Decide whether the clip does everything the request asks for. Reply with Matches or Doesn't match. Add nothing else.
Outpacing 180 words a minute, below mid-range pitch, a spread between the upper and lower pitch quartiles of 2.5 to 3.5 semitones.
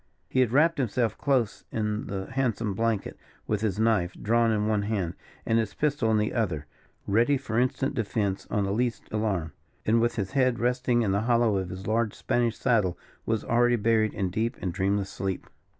Matches